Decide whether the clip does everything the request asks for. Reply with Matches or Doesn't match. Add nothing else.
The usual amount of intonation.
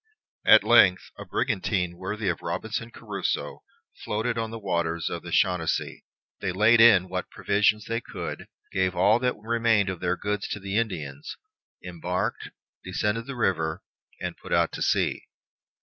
Matches